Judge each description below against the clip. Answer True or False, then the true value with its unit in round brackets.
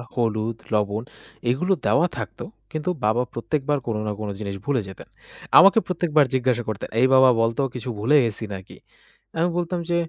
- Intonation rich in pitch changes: True (5.7 semitones)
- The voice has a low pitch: True (125 Hz)